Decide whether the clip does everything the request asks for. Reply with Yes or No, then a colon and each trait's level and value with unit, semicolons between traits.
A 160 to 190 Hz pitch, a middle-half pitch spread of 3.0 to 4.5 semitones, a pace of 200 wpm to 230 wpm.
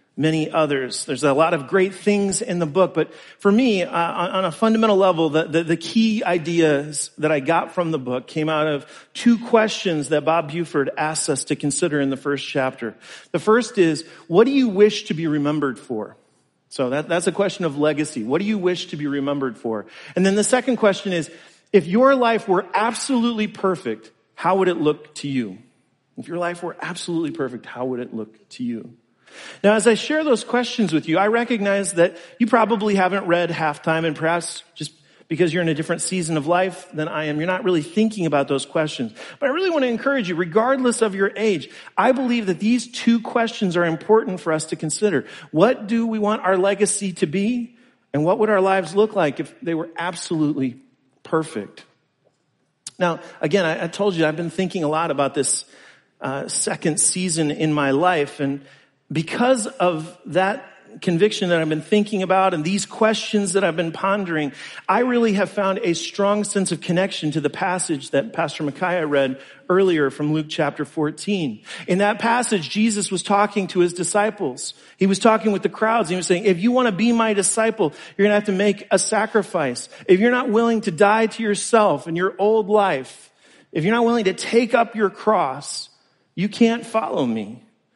No: medium, 185 Hz; average, 5.1 semitones; fast, 205 wpm